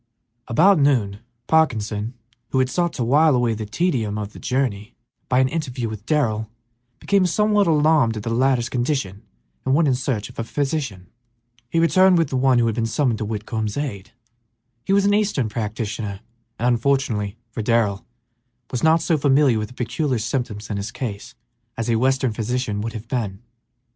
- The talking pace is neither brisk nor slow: Yes, average, 180 wpm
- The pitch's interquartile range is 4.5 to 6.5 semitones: Yes, average, 4.9 semitones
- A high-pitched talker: No, low, 120 Hz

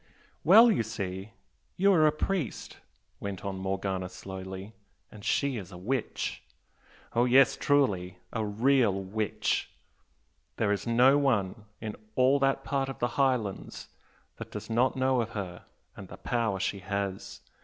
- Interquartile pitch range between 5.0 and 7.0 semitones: Yes, wide, 5.5 semitones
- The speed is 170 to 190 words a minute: No, average, 150 wpm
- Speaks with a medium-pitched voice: No, low, 110 Hz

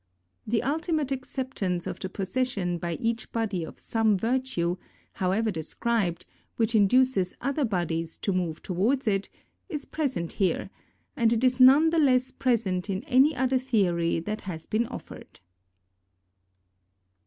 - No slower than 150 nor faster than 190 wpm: No, average, 140 wpm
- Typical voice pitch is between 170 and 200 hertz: No, high, 225 Hz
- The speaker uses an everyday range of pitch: No, wide, 6.0 semitones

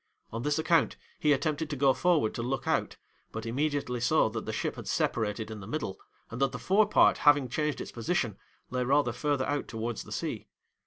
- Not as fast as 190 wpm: No, fast, 205 wpm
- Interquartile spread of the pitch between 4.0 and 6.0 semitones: Yes, average, 4.4 semitones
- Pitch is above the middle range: No, low, 135 Hz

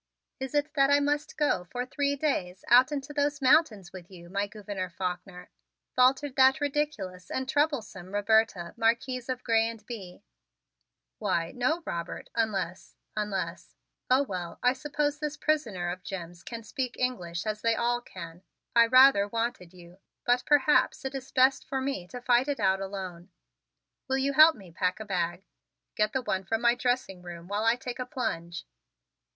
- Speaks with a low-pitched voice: No, high, 230 Hz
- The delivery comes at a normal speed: Yes, average, 170 wpm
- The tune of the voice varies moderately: No, wide, 6.2 semitones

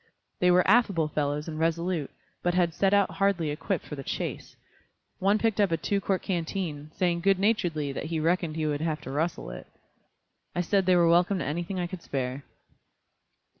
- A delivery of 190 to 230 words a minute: Yes, average, 195 wpm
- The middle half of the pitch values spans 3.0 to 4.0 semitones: Yes, average, 3.6 semitones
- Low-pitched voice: No, medium, 170 Hz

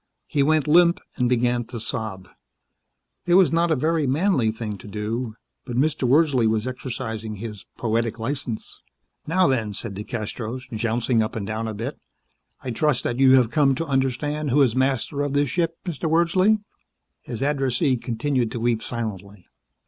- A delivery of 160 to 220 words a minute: Yes, average, 170 wpm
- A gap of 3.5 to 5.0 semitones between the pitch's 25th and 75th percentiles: Yes, average, 4.6 semitones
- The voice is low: Yes, low, 125 Hz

